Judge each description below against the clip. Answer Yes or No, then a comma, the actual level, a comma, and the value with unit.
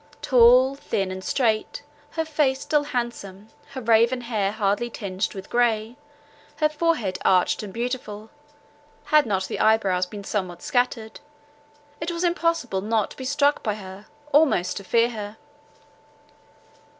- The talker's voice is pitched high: Yes, high, 230 Hz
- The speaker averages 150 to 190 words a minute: No, average, 140 wpm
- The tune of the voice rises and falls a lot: Yes, wide, 5.8 semitones